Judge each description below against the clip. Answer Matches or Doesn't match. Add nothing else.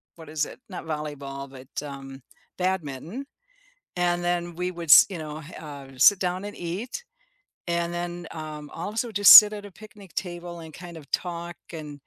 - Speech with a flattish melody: Doesn't match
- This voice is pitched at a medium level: Matches